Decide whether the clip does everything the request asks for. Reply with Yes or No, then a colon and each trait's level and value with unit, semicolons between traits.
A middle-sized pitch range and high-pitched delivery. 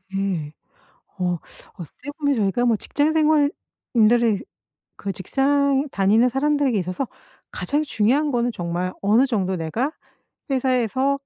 No: wide, 6.3 semitones; high, 240 Hz